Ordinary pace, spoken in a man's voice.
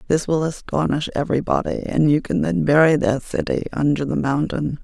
No: average, 175 wpm; female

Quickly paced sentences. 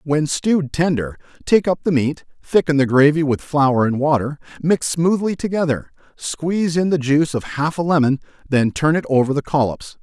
No: average, 185 wpm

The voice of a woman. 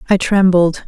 Yes: female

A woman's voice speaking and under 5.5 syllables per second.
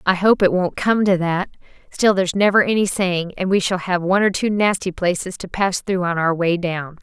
Yes: female; 5.3 syllables/s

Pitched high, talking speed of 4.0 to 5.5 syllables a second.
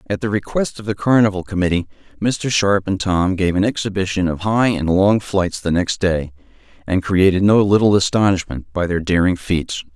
No: very low, 95 Hz; 5.1 syllables/s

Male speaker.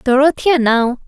No: female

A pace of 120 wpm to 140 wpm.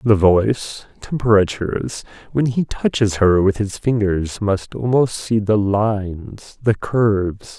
Yes: slow, 135 wpm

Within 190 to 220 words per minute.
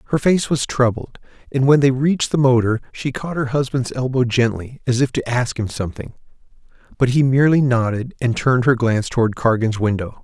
Yes: average, 195 wpm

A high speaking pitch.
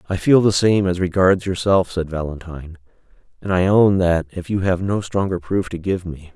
No: very low, 90 Hz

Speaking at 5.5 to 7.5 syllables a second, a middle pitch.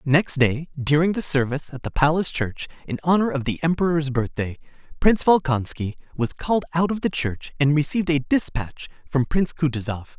Yes: 5.7 syllables/s; medium, 150 Hz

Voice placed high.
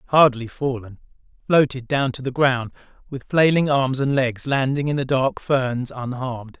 No: low, 130 Hz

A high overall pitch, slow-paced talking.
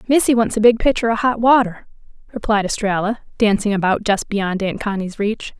No: high, 215 Hz; average, 180 wpm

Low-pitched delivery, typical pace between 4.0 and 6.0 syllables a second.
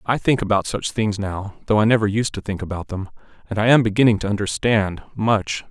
Yes: low, 105 Hz; 5.6 syllables/s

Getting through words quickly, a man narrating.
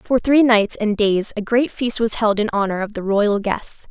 No: fast, 245 wpm; female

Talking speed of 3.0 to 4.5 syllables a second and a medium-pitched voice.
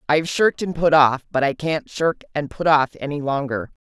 No: 5.3 syllables/s; medium, 150 Hz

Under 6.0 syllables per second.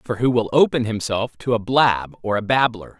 Yes: 4.9 syllables/s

